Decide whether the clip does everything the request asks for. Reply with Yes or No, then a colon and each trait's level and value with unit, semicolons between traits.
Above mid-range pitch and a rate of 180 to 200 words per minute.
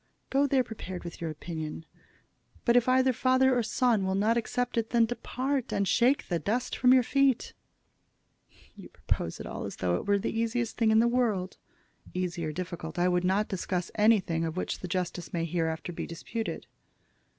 Yes: high, 205 Hz; average, 190 wpm